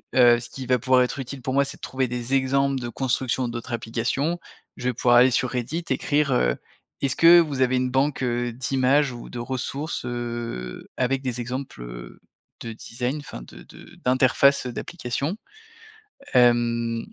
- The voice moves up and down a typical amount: No, narrow, 2.1 semitones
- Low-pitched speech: Yes, low, 125 Hz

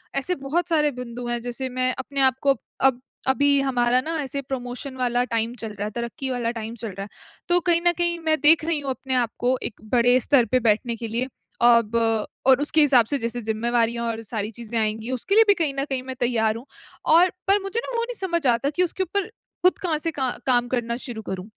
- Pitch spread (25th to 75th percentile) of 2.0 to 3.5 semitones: No, average, 4.0 semitones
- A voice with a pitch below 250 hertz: No, very high, 255 Hz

